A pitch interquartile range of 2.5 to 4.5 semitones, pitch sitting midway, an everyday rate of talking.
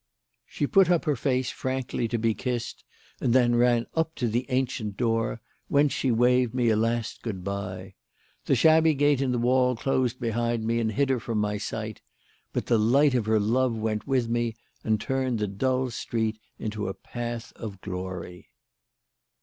No: average, 2.9 semitones; low, 120 Hz; average, 180 wpm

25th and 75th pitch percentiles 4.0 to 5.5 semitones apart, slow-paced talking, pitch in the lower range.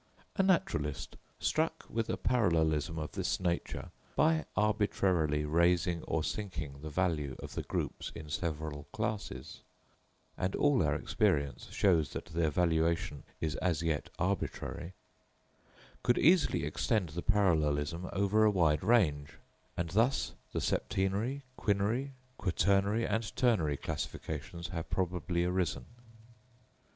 Yes: average, 5.1 semitones; slow, 120 wpm; very low, 90 Hz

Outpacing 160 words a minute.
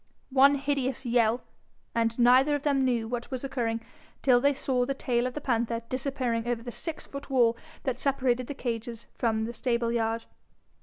Yes: average, 175 wpm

